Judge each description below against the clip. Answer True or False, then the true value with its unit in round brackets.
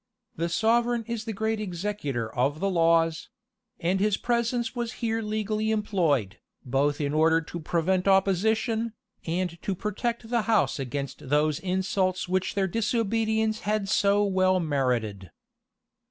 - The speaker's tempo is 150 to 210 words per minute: False (140 wpm)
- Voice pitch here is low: False (190 Hz)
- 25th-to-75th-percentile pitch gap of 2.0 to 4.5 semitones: False (5.1 semitones)